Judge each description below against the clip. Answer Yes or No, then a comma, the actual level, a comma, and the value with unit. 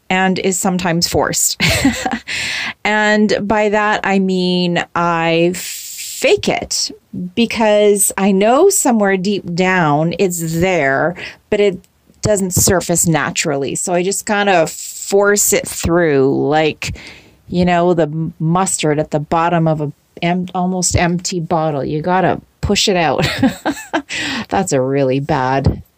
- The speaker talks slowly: Yes, slow, 130 wpm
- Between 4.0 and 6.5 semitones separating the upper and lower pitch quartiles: No, average, 3.5 semitones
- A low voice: No, medium, 180 Hz